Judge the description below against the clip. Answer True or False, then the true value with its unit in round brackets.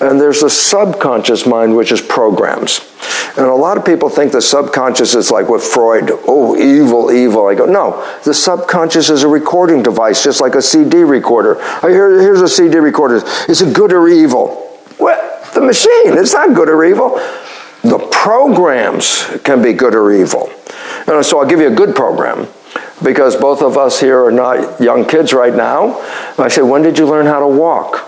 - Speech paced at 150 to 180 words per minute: False (195 wpm)